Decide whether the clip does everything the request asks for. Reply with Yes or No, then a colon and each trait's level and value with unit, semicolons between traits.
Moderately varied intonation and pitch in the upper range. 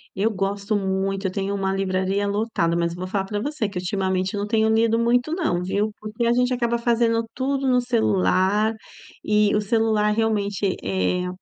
Yes: average, 3.0 semitones; high, 210 Hz